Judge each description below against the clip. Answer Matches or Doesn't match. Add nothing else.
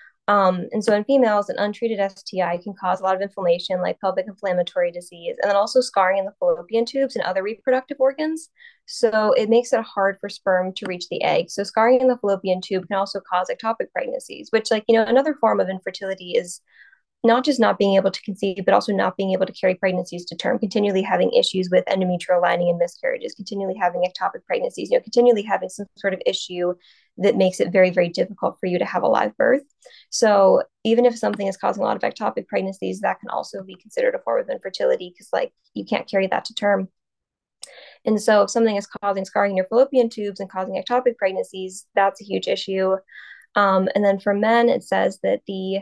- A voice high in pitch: Matches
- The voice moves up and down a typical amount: Matches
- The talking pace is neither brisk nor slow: Doesn't match